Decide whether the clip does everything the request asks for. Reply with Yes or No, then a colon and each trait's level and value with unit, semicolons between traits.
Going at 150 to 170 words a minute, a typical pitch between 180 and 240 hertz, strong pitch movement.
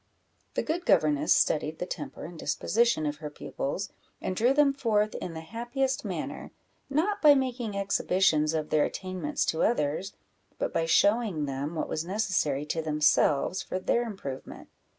Yes: average, 160 wpm; medium, 185 Hz; wide, 7.4 semitones